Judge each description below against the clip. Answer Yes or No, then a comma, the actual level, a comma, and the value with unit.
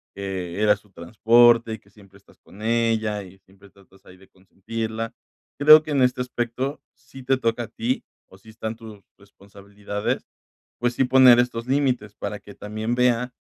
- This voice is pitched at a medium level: No, low, 110 Hz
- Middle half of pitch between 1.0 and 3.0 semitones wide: No, average, 3.6 semitones